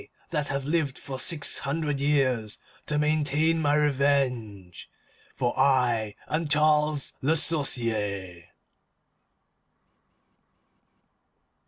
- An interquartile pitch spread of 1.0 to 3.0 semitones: No, average, 3.7 semitones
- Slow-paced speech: Yes, slow, 85 wpm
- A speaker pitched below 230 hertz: Yes, medium, 140 Hz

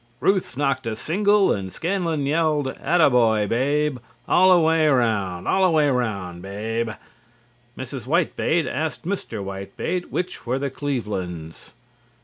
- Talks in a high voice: No, low, 135 Hz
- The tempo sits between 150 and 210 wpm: No, slow, 135 wpm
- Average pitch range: No, wide, 7.0 semitones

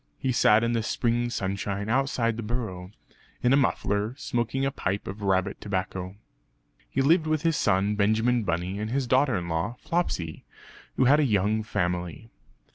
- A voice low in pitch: Yes, low, 110 Hz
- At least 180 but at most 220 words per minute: No, average, 170 wpm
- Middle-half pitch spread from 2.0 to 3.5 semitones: No, average, 4.6 semitones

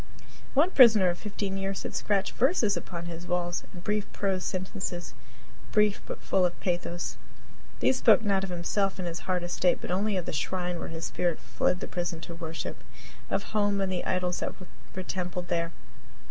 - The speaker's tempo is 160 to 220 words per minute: Yes, average, 190 wpm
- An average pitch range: No, narrow, 2.3 semitones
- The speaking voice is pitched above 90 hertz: Yes, medium, 185 Hz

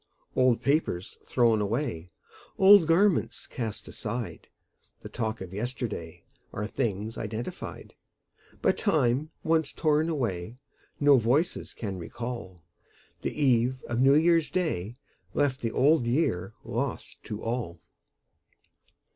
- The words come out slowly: Yes, slow, 115 wpm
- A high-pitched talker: No, low, 120 Hz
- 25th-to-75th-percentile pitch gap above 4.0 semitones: Yes, wide, 5.5 semitones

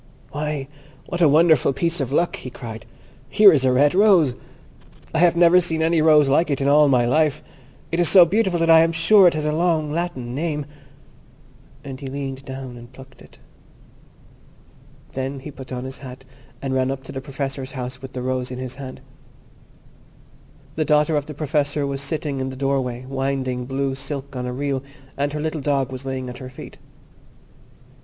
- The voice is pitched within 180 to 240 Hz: No, medium, 140 Hz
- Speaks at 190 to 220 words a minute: Yes, average, 195 wpm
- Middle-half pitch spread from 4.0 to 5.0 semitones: No, average, 3.0 semitones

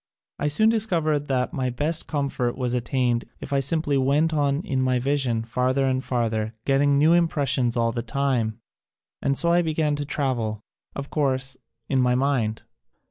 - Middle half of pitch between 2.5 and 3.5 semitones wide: Yes, average, 2.8 semitones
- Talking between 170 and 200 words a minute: Yes, average, 180 wpm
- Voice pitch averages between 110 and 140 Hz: Yes, low, 135 Hz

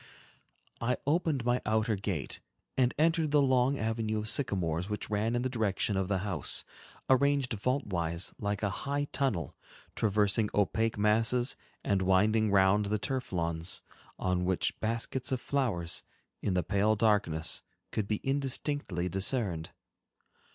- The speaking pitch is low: Yes, low, 110 Hz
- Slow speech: No, average, 145 wpm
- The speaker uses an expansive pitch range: No, average, 4.9 semitones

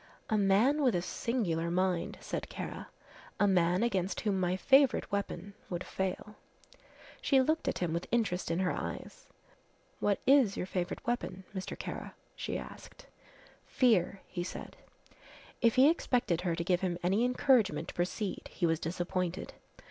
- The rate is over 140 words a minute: Yes, average, 155 wpm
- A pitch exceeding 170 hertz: Yes, high, 190 Hz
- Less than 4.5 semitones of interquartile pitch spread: No, average, 5.0 semitones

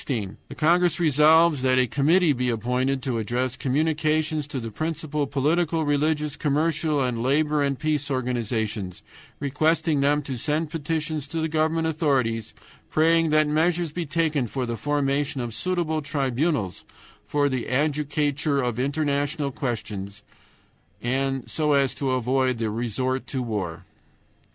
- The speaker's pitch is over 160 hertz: No, medium, 145 Hz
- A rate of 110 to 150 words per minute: Yes, slow, 135 wpm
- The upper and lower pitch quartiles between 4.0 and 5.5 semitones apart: No, average, 3.5 semitones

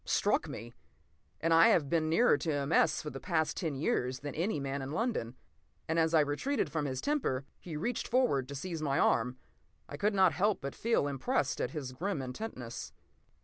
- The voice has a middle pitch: Yes, medium, 150 Hz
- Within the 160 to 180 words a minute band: No, average, 200 wpm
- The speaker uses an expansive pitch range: No, average, 4.8 semitones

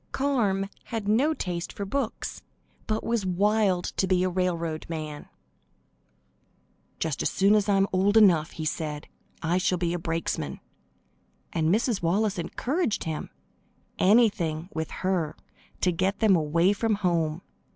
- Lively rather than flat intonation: No, average, 4.0 semitones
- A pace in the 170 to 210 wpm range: No, average, 145 wpm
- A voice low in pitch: No, medium, 185 Hz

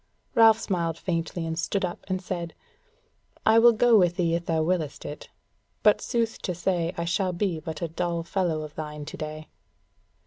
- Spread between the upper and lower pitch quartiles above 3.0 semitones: No, narrow, 2.6 semitones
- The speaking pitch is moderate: Yes, medium, 170 Hz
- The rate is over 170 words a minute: Yes, average, 185 wpm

